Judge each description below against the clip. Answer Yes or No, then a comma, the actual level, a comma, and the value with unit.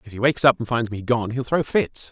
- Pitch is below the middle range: Yes, low, 120 Hz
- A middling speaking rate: No, fast, 315 wpm